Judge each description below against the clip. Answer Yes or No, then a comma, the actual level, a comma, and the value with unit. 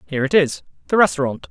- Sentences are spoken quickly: No, average, 160 wpm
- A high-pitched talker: No, medium, 155 Hz